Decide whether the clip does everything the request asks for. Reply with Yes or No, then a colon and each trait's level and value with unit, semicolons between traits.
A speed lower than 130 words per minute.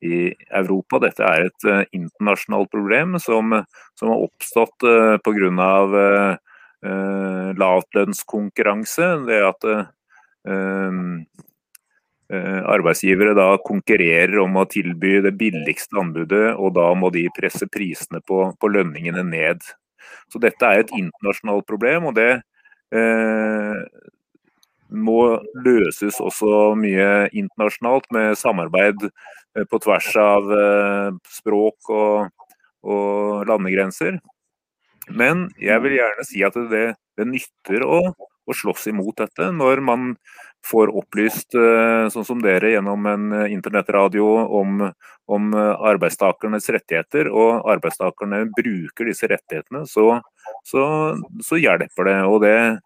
Yes: average, 115 wpm